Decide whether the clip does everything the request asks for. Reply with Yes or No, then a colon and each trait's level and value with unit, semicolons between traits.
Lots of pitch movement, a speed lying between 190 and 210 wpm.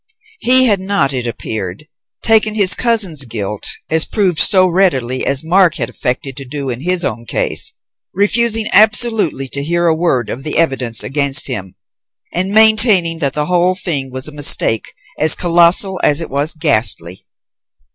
No: wide, 6.1 semitones; average, 165 wpm